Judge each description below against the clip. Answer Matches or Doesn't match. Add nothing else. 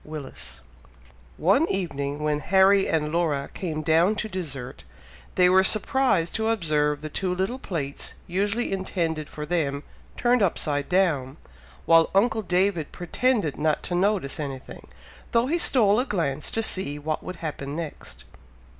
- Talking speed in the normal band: Matches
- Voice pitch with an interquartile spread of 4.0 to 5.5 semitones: Matches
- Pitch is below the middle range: Doesn't match